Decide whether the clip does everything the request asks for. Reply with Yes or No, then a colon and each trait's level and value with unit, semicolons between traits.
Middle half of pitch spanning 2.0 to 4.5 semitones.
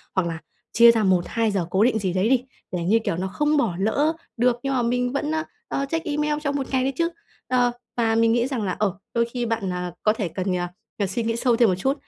No: average, 5.3 semitones